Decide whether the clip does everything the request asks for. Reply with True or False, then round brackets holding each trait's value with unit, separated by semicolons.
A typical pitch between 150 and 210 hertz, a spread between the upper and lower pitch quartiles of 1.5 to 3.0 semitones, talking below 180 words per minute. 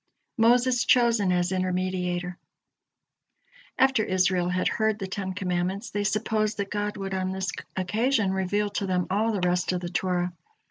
True (190 Hz; 2.7 semitones; 155 wpm)